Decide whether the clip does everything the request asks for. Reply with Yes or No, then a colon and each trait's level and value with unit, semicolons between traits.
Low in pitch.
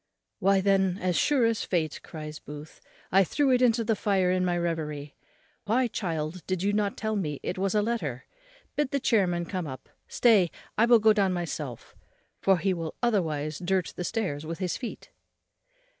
No: medium, 185 Hz